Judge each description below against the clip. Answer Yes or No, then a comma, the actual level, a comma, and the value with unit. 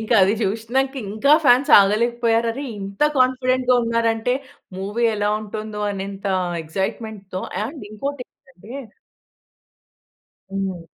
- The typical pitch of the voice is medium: No, high, 225 Hz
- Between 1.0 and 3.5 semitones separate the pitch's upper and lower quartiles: No, average, 3.9 semitones